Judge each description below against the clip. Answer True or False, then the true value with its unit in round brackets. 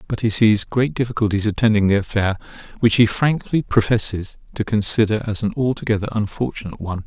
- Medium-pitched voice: False (110 Hz)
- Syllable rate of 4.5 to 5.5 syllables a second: False (6.1 syllables/s)